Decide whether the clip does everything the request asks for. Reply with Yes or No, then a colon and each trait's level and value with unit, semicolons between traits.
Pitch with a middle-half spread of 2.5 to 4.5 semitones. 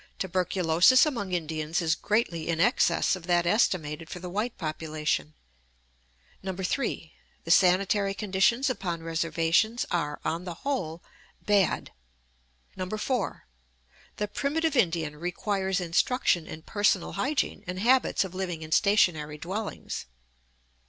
Yes: average, 4.1 semitones